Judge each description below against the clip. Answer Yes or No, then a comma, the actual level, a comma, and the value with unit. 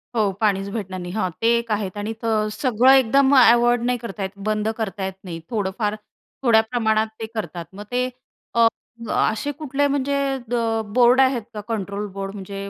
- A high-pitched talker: Yes, high, 220 Hz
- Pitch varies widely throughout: No, average, 3.3 semitones